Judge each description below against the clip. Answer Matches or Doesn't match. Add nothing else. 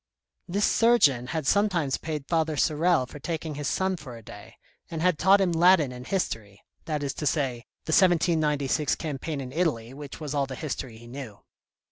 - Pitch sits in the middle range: Matches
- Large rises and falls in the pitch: Doesn't match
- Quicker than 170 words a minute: Matches